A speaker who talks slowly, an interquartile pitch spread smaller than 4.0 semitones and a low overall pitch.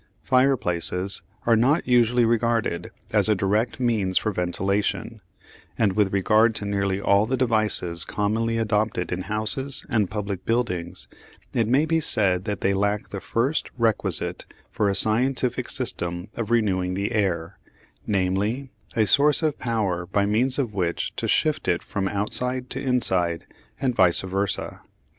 No: average, 150 wpm; average, 3.6 semitones; low, 105 Hz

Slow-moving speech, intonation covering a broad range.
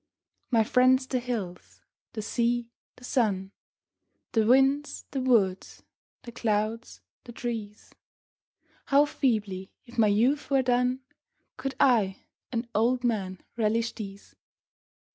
No: slow, 120 wpm; average, 3.2 semitones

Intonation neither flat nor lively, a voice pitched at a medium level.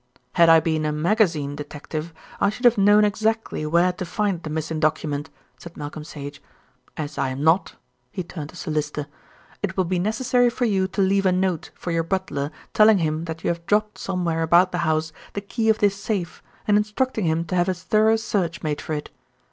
Yes: average, 4.6 semitones; medium, 175 Hz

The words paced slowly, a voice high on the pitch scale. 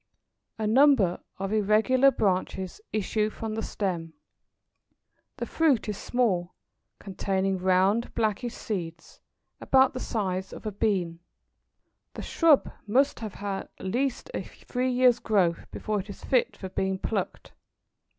Yes: slow, 130 wpm; high, 210 Hz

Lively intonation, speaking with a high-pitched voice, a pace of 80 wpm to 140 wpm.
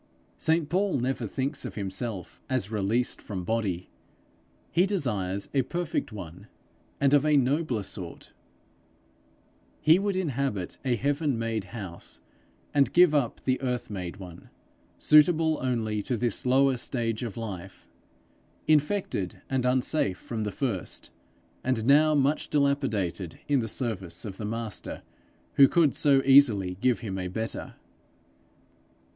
No: wide, 5.7 semitones; low, 125 Hz; slow, 135 wpm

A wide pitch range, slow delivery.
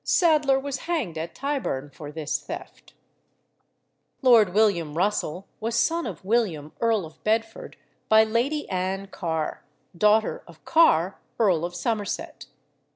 Yes: wide, 6.0 semitones; slow, 130 wpm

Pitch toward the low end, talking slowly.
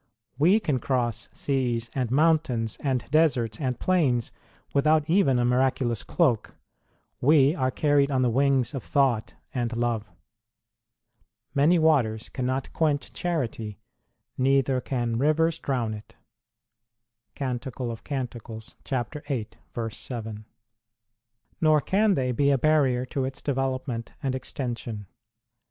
Yes: low, 130 Hz; slow, 115 wpm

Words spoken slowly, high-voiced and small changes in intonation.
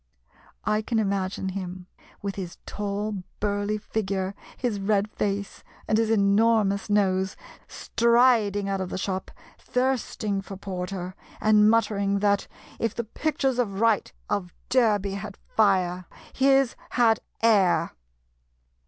Yes: slow, 125 wpm; high, 205 Hz; narrow, 2.2 semitones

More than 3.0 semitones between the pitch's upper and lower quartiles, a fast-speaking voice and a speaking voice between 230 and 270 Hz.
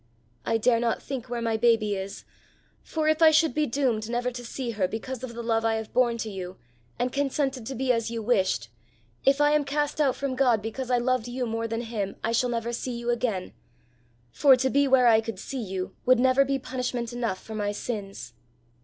No: average, 2.7 semitones; fast, 225 wpm; high, 240 Hz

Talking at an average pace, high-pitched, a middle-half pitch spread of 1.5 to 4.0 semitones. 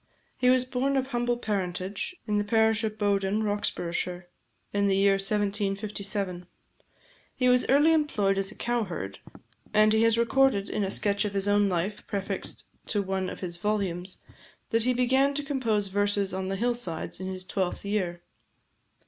Yes: average, 170 wpm; high, 205 Hz; average, 3.4 semitones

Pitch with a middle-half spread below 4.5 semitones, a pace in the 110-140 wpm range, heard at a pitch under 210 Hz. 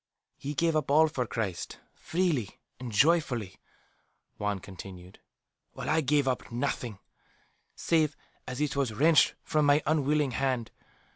No: average, 4.8 semitones; slow, 135 wpm; medium, 140 Hz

